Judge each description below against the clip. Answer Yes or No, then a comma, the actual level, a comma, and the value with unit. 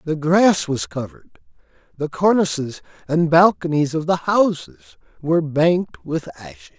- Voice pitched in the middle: Yes, medium, 160 Hz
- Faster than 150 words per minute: No, slow, 135 wpm